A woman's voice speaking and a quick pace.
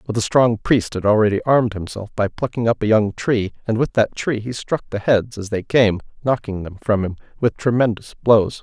No: male; fast, 215 wpm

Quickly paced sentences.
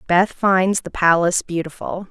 No: average, 145 wpm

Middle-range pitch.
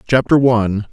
No: low, 120 Hz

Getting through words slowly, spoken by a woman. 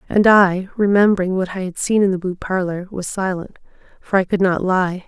No: average, 200 wpm; female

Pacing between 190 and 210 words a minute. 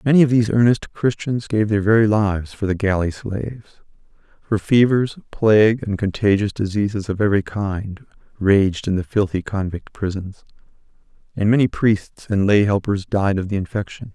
No: average, 160 wpm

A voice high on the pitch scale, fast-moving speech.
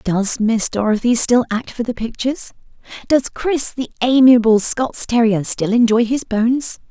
No: high, 235 Hz; average, 155 wpm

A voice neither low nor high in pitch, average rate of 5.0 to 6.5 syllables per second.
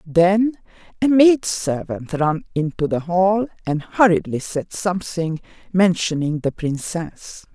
No: medium, 180 Hz; 3.7 syllables/s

